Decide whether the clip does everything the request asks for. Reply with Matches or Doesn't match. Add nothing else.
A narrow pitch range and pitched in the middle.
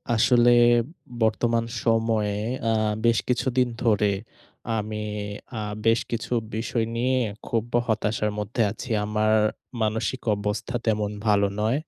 Doesn't match